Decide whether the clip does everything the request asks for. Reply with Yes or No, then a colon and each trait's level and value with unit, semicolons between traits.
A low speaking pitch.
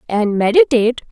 No: high, 235 Hz